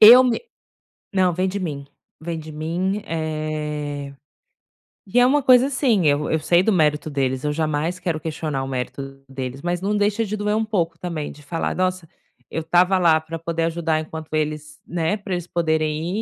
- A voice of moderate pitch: Yes, medium, 165 Hz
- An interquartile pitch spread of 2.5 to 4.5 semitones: Yes, average, 3.6 semitones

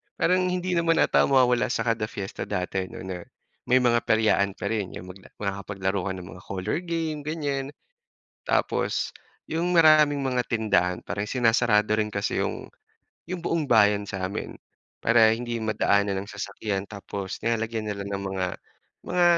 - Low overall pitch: Yes, low, 110 Hz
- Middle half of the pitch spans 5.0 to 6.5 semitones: Yes, wide, 5.6 semitones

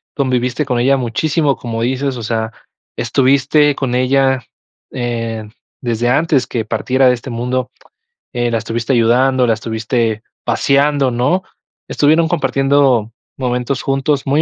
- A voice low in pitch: Yes, low, 125 Hz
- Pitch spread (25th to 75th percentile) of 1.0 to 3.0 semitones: Yes, average, 2.7 semitones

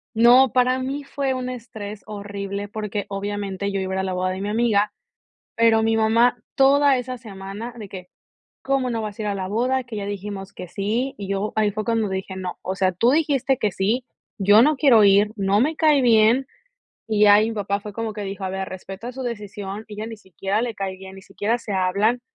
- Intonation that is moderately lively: Yes, average, 3.3 semitones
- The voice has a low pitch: No, high, 210 Hz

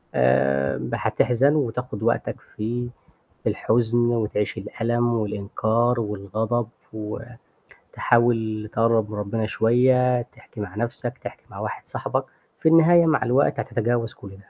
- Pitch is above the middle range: No, low, 115 Hz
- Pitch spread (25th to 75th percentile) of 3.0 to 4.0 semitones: No, narrow, 2.4 semitones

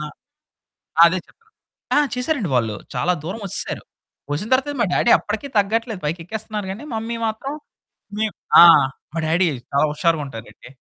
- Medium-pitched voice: No, high, 205 Hz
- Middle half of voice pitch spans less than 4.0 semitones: No, wide, 5.6 semitones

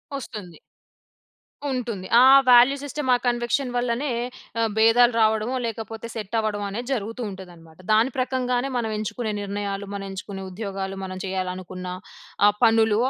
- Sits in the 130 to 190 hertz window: No, high, 220 Hz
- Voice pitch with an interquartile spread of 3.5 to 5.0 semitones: Yes, average, 3.8 semitones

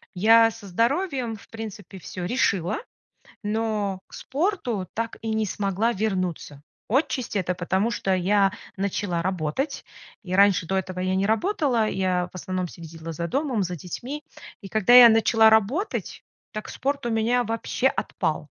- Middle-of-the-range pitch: No, high, 210 Hz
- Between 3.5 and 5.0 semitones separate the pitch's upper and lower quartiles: Yes, average, 4.0 semitones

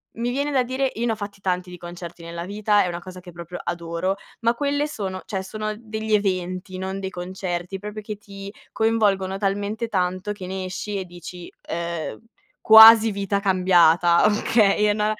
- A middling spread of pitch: Yes, average, 3.0 semitones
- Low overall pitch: No, high, 195 Hz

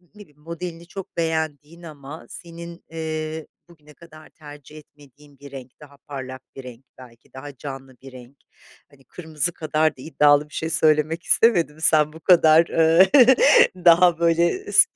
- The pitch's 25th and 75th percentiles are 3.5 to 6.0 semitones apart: No, narrow, 2.6 semitones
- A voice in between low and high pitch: Yes, medium, 155 Hz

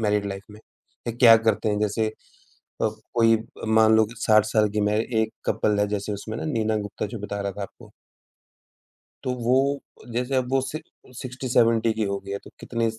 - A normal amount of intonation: No, narrow, 2.3 semitones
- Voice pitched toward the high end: No, low, 110 Hz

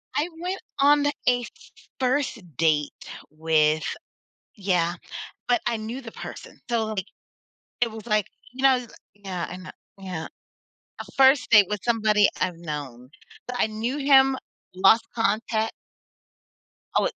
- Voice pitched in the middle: No, high, 220 Hz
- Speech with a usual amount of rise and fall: No, wide, 5.7 semitones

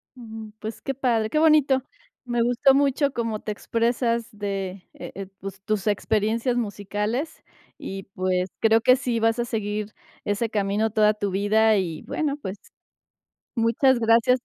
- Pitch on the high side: Yes, high, 220 Hz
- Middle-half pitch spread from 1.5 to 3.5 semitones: Yes, average, 2.9 semitones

